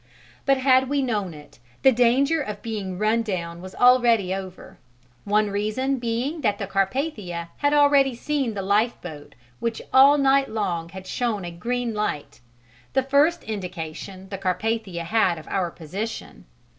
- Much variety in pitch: Yes, wide, 5.7 semitones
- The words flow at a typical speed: Yes, average, 155 wpm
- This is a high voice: Yes, high, 215 Hz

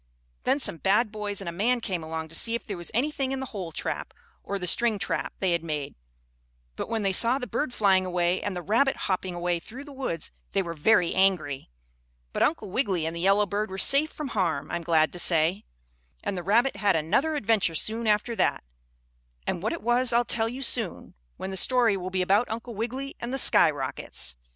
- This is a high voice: Yes, high, 200 Hz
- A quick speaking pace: Yes, fast, 215 wpm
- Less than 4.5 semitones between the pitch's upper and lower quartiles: No, average, 5.3 semitones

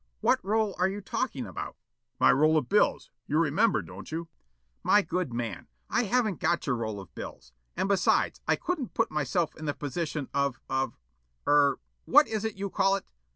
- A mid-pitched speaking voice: Yes, medium, 165 Hz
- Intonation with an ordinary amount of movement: No, wide, 6.9 semitones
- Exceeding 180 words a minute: Yes, average, 190 wpm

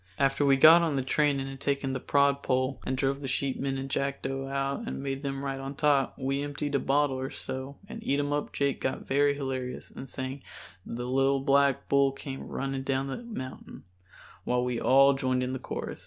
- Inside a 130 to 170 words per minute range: No, fast, 205 wpm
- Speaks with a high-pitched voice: No, low, 135 Hz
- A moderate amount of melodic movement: No, narrow, 0.9 semitones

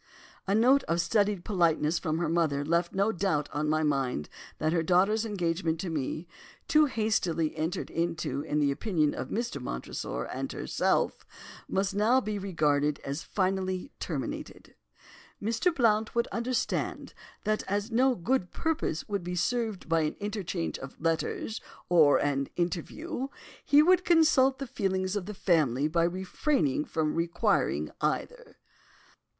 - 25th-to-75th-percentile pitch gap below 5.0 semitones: No, wide, 5.6 semitones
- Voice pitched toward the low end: No, medium, 180 Hz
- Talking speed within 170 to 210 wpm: No, average, 145 wpm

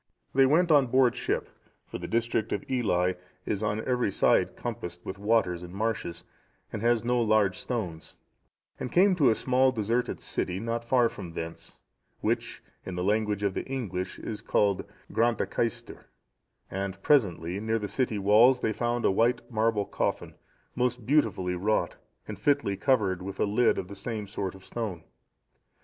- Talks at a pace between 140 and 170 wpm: Yes, average, 165 wpm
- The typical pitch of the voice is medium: No, low, 110 Hz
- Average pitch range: Yes, average, 3.8 semitones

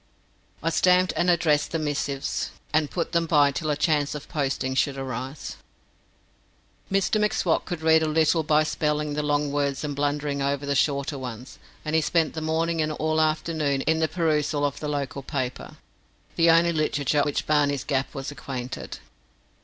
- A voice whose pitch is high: No, medium, 150 Hz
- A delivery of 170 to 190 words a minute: Yes, average, 175 wpm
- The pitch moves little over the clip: Yes, narrow, 2.1 semitones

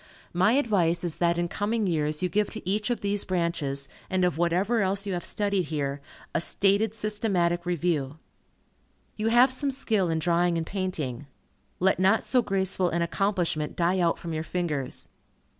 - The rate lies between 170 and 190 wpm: Yes, average, 175 wpm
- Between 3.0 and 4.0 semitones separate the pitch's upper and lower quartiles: Yes, average, 3.3 semitones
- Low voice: No, medium, 180 Hz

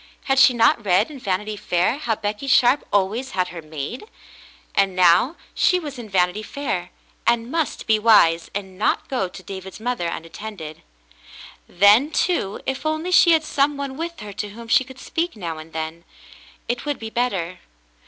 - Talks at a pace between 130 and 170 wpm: No, average, 180 wpm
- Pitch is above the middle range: Yes, high, 215 Hz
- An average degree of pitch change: No, wide, 6.3 semitones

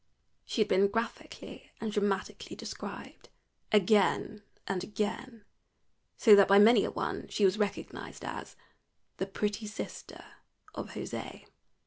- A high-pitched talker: Yes, high, 210 Hz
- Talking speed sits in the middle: No, slow, 125 wpm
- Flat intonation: Yes, narrow, 1.4 semitones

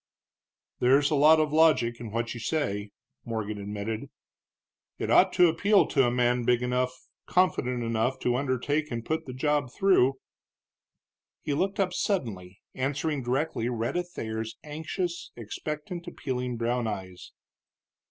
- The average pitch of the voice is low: Yes, low, 125 Hz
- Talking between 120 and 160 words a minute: Yes, average, 140 wpm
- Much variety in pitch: No, average, 5.0 semitones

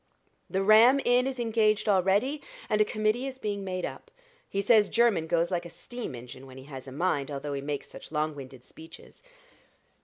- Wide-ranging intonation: Yes, wide, 7.2 semitones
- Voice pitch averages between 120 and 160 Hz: No, high, 190 Hz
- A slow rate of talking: No, average, 195 wpm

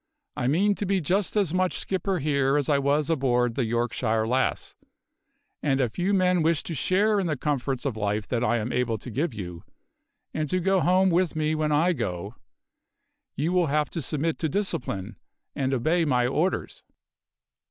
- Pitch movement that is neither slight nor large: No, wide, 6.3 semitones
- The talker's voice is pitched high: No, medium, 150 Hz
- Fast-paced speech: No, average, 185 wpm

